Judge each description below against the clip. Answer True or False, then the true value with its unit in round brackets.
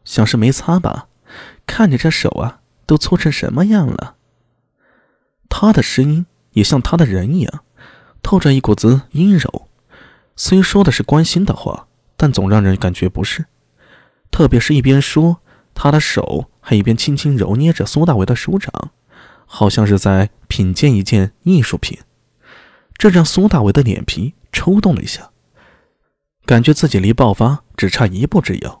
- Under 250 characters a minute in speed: True (230 characters per minute)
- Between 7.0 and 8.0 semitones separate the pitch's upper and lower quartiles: True (7.4 semitones)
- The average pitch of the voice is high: False (140 Hz)